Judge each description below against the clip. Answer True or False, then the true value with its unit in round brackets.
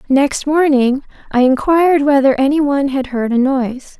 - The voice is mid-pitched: False (275 Hz)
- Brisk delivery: False (165 wpm)